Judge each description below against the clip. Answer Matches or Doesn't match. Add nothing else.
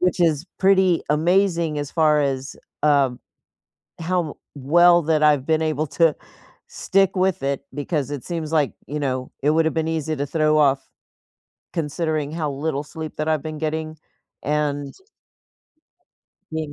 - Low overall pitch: Doesn't match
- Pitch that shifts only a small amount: Matches